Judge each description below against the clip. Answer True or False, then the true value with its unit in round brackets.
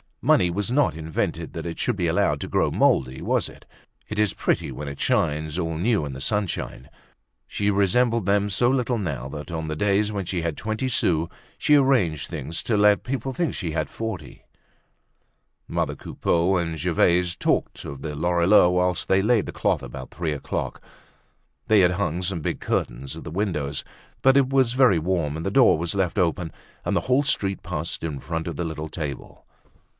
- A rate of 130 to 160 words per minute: False (195 wpm)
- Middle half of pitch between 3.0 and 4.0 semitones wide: False (5.0 semitones)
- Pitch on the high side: False (90 Hz)